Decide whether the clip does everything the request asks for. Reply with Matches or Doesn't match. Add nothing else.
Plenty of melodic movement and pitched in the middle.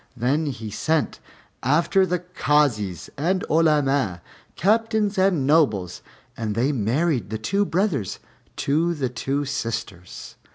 Matches